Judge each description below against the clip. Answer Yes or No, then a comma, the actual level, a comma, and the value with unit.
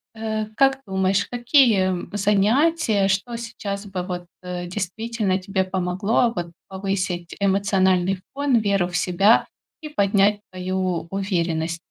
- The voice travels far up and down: No, average, 2.9 semitones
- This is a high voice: Yes, high, 195 Hz